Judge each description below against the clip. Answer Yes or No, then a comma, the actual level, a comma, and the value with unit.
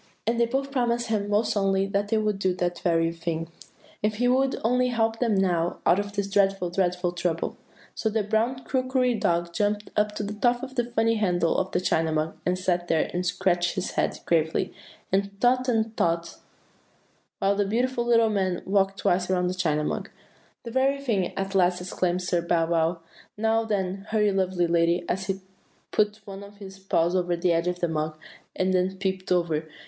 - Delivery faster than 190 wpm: Yes, fast, 205 wpm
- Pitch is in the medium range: No, high, 195 Hz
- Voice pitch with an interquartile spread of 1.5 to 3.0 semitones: No, average, 3.8 semitones